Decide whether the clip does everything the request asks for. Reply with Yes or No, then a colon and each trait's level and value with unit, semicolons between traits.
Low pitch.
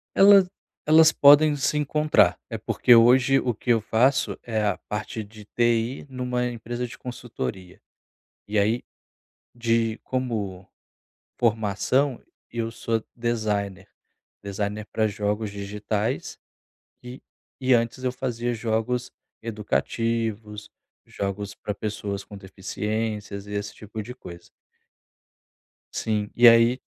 Yes: low, 115 Hz